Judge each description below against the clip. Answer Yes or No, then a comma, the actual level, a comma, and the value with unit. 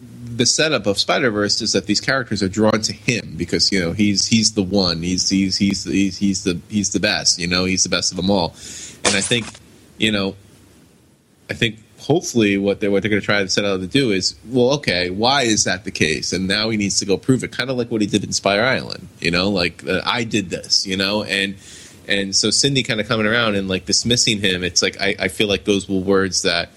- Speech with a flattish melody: Yes, narrow, 2.2 semitones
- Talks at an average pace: No, fast, 255 wpm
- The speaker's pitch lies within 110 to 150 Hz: No, low, 100 Hz